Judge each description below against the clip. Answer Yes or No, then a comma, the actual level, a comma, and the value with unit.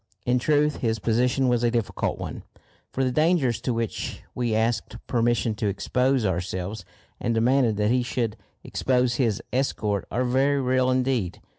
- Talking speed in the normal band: Yes, average, 160 wpm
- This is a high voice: No, low, 120 Hz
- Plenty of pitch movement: No, narrow, 2.6 semitones